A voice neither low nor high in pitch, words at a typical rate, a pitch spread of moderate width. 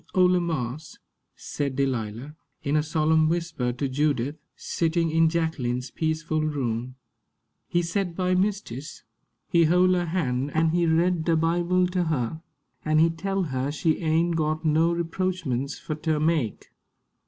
Yes: medium, 160 Hz; average, 145 wpm; average, 3.2 semitones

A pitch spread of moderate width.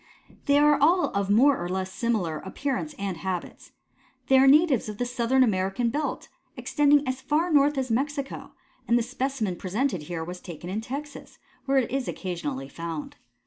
No: wide, 6.9 semitones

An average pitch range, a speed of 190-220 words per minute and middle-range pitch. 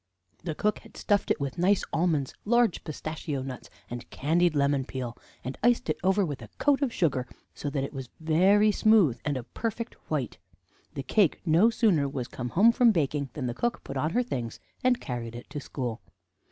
No: wide, 7.5 semitones; average, 200 wpm; medium, 155 Hz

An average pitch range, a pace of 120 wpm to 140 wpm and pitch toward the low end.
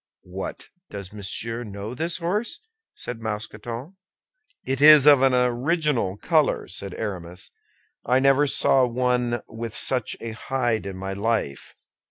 Yes: average, 4.4 semitones; slow, 135 wpm; low, 120 Hz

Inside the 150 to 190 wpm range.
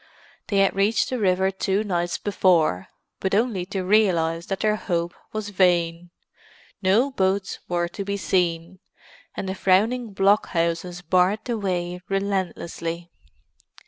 No: slow, 135 wpm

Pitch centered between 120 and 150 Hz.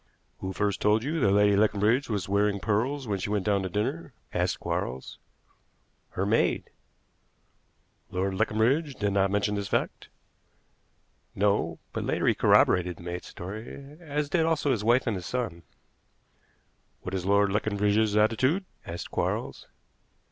No: low, 105 Hz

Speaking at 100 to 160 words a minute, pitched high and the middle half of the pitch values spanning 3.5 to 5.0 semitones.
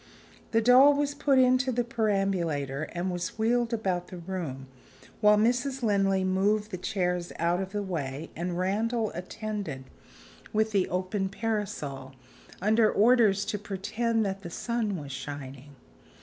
Yes: average, 145 wpm; high, 195 Hz; average, 4.2 semitones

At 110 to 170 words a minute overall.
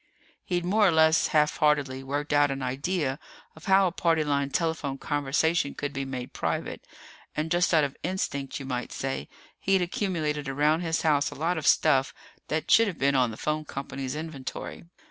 No: average, 185 wpm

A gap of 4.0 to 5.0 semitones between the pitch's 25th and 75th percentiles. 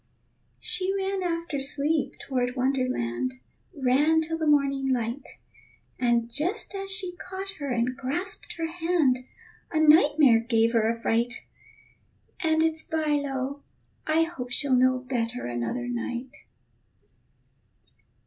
Yes: average, 4.6 semitones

